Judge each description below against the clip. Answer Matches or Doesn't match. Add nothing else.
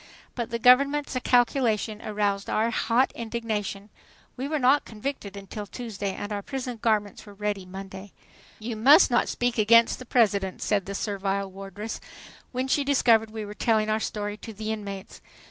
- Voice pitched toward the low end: Doesn't match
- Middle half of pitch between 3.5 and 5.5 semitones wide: Doesn't match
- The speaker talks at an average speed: Matches